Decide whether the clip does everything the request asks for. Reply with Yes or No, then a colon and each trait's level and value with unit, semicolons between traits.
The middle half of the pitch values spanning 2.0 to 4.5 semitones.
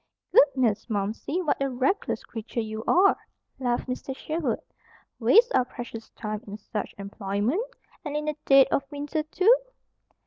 No: wide, 5.5 semitones